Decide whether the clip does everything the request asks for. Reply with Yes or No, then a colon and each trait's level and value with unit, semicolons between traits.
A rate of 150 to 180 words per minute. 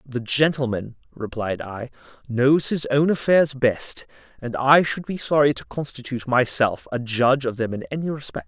Yes: average, 170 wpm